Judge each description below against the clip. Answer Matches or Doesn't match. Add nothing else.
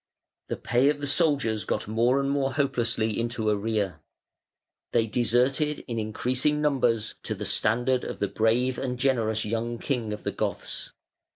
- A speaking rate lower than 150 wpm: Doesn't match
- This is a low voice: Matches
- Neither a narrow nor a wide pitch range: Matches